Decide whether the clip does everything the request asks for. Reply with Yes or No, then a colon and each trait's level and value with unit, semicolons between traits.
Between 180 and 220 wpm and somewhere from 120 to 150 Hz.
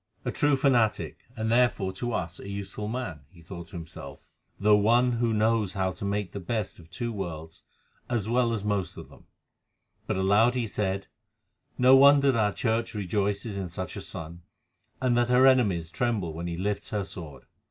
No: average, 190 wpm; low, 105 Hz